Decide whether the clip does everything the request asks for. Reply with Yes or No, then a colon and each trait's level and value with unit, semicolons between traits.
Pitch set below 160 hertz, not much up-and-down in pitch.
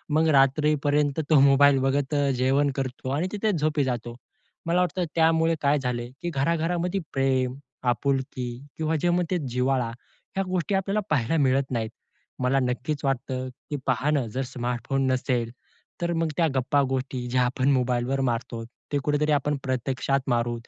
No: low, 135 Hz; average, 3.2 semitones